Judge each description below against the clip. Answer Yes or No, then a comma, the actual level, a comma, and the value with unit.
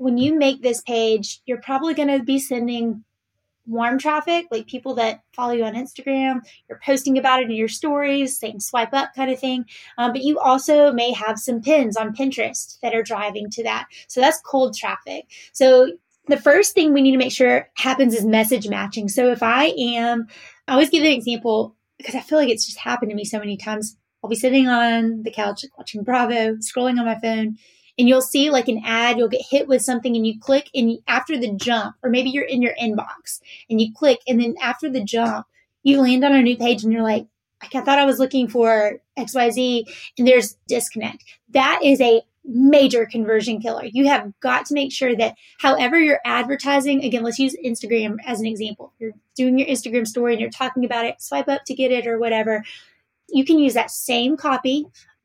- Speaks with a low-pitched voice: No, high, 245 Hz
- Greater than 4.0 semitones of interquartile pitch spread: No, average, 2.9 semitones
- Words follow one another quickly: Yes, fast, 210 wpm